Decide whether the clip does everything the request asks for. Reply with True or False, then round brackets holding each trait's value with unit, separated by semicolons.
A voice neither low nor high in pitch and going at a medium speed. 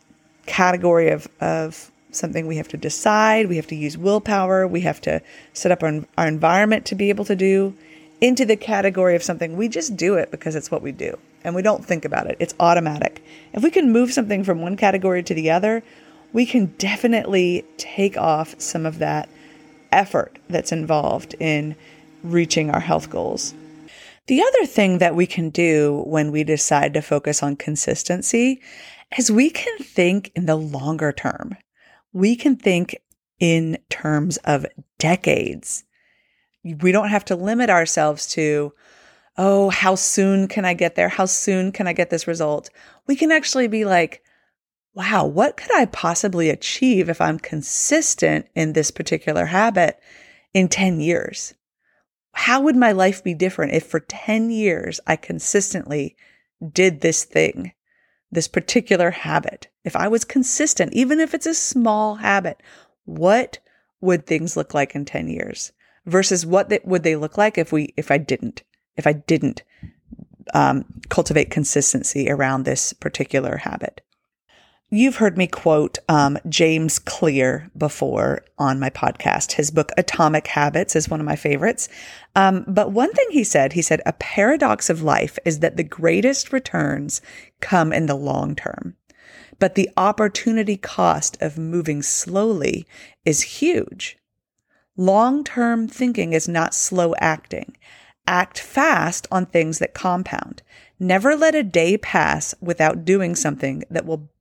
True (180 Hz; 160 wpm)